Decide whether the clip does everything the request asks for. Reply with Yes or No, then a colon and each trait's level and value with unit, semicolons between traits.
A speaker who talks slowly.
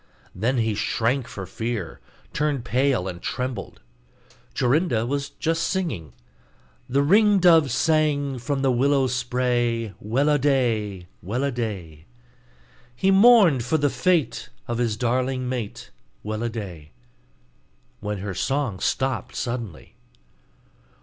Yes: slow, 125 wpm